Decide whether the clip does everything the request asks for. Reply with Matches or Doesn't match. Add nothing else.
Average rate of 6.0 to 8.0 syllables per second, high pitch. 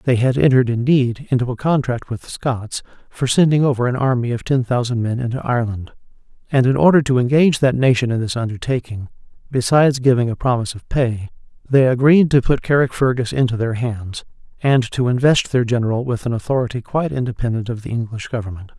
Doesn't match